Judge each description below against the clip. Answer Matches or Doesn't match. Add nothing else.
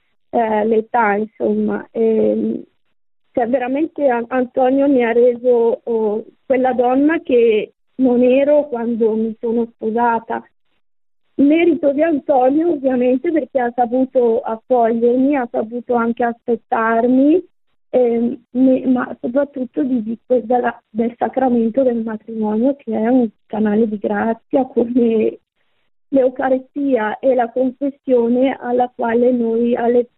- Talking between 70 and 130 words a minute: Matches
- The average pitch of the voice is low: Doesn't match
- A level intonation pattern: Matches